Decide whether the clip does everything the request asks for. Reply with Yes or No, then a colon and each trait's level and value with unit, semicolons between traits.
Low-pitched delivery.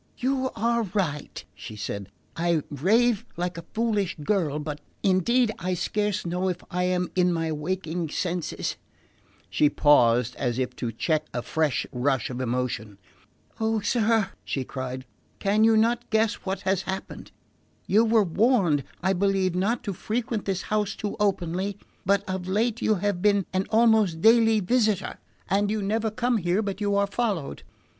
No: high, 190 Hz